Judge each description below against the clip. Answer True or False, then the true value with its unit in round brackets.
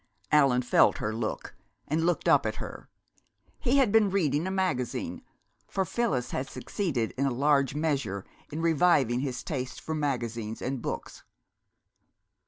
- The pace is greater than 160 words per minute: False (150 wpm)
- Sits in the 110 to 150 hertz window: True (140 Hz)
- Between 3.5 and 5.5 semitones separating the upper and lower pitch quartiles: True (5.2 semitones)